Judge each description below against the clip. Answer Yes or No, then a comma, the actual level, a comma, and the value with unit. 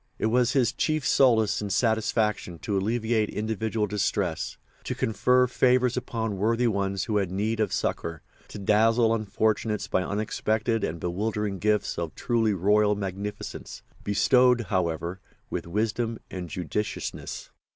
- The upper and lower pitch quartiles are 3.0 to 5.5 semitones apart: No, narrow, 2.5 semitones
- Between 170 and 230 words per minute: No, slow, 135 wpm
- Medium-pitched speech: No, low, 105 Hz